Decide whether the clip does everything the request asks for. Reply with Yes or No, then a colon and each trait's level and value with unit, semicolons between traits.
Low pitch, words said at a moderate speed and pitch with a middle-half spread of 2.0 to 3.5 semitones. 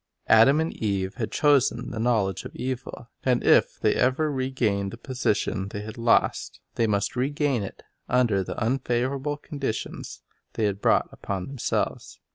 No: low, 120 Hz; average, 155 wpm; average, 4.2 semitones